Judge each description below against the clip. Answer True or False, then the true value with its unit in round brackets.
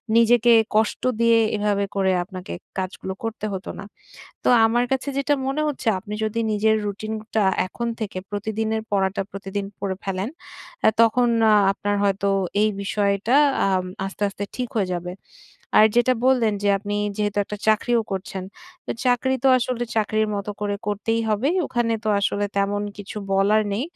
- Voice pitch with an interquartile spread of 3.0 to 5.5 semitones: False (2.5 semitones)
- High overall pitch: True (210 Hz)